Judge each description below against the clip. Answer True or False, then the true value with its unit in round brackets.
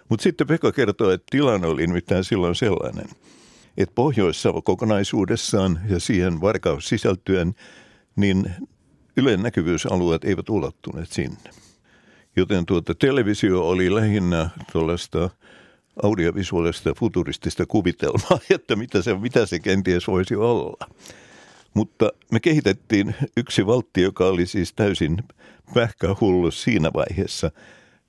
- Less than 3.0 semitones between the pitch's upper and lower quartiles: True (2.4 semitones)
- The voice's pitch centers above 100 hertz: False (95 Hz)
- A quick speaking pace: False (110 wpm)